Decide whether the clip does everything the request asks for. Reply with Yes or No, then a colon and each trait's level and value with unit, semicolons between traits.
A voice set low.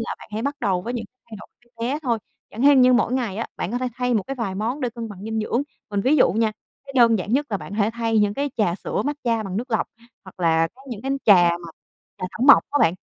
No: high, 230 Hz